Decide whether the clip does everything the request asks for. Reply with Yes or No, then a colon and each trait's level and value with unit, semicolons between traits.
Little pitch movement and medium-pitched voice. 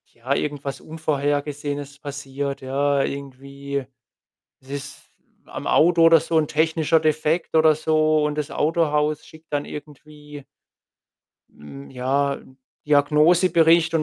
Yes: narrow, 2.0 semitones; medium, 150 Hz